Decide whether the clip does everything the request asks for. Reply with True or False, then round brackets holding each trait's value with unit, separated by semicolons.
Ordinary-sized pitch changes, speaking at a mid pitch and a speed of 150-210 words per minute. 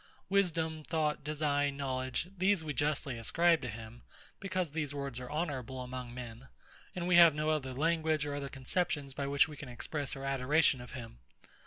True (3.6 semitones; 145 Hz; 180 wpm)